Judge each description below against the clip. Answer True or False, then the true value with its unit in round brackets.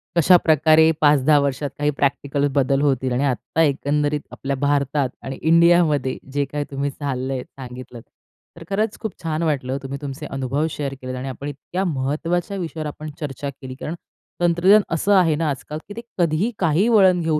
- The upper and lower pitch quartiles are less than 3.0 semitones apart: False (3.3 semitones)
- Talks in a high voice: False (145 Hz)